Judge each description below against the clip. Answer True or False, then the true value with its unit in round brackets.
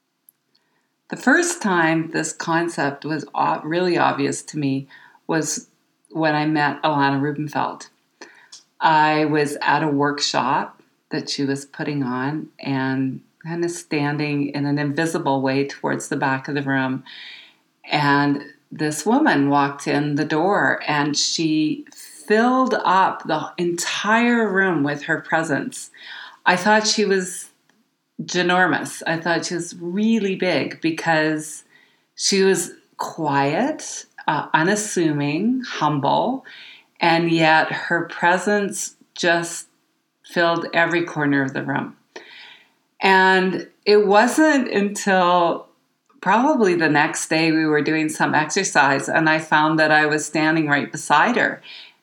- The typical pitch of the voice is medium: True (160 Hz)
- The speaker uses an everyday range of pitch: True (4.6 semitones)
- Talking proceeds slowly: True (125 wpm)